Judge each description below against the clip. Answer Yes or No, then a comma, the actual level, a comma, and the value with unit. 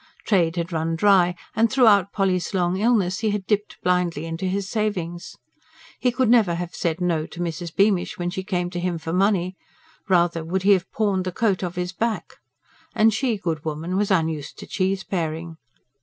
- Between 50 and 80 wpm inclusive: No, average, 185 wpm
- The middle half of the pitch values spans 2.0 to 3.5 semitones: Yes, average, 2.9 semitones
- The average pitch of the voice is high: No, medium, 180 Hz